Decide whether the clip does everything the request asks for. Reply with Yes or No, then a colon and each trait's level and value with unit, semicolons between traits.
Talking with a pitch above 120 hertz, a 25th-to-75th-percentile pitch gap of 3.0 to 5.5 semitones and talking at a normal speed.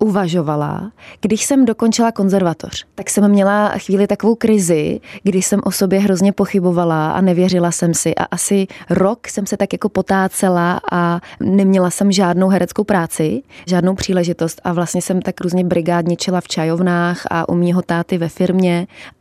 No: medium, 185 Hz; narrow, 2.4 semitones; average, 160 wpm